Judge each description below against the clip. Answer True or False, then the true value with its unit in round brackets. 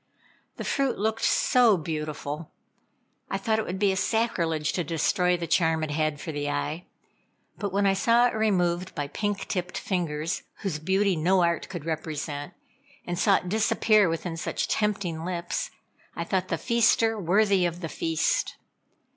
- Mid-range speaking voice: True (180 Hz)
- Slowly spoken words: False (165 wpm)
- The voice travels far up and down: False (4.2 semitones)